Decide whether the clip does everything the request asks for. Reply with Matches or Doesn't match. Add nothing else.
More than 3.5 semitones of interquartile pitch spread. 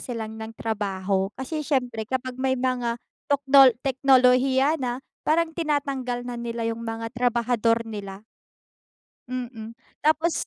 Doesn't match